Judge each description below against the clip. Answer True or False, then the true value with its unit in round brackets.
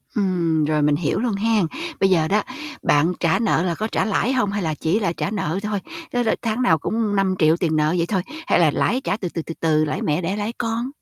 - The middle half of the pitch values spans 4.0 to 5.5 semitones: True (5.1 semitones)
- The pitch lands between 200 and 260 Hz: False (185 Hz)